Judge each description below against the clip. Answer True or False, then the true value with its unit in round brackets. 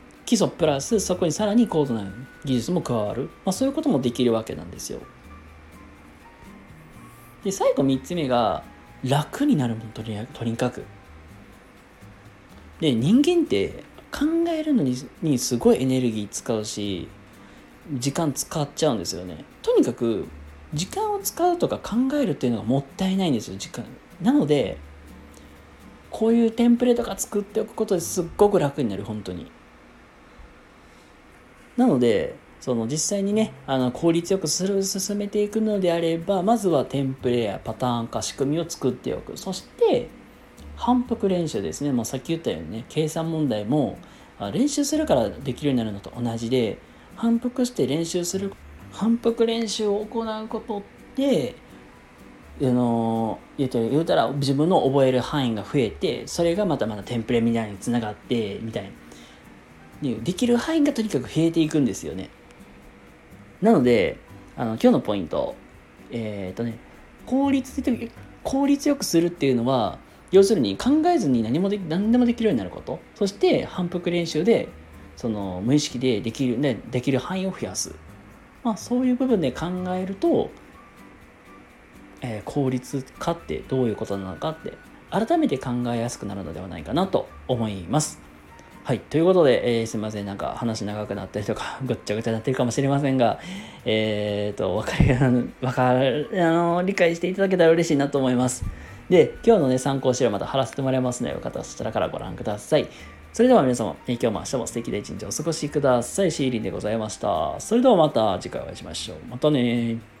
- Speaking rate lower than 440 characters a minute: True (345 characters per minute)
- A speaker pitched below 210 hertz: True (140 Hz)